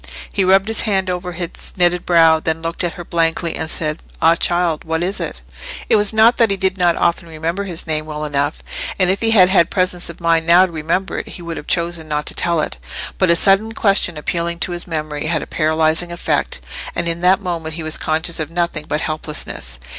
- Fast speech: Yes, fast, 230 wpm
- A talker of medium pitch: Yes, medium, 170 Hz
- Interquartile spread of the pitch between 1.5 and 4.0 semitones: Yes, narrow, 2.4 semitones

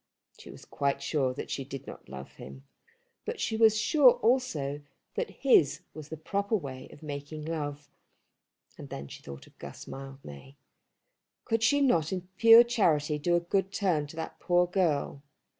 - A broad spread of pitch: Yes, wide, 6.2 semitones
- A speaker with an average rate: Yes, average, 175 wpm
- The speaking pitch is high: No, medium, 155 Hz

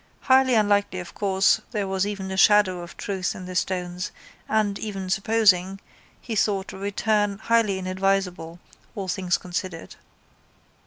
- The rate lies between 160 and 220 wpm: No, average, 145 wpm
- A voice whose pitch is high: Yes, high, 195 Hz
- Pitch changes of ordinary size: No, narrow, 2.0 semitones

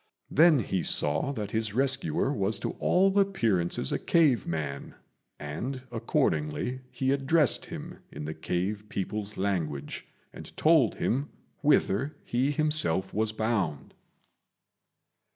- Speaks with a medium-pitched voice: No, low, 110 Hz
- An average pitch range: No, wide, 7.0 semitones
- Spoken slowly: Yes, slow, 120 wpm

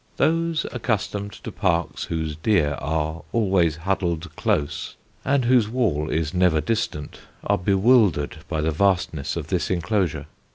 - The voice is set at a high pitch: No, very low, 90 Hz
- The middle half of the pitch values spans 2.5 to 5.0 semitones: No, wide, 5.4 semitones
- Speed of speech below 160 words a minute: Yes, slow, 135 wpm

